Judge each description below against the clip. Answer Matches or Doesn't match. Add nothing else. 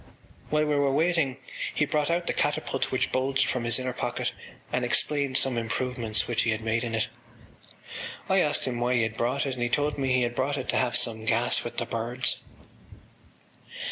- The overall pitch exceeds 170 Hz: Doesn't match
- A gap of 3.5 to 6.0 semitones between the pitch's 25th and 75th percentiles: Doesn't match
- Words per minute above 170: Matches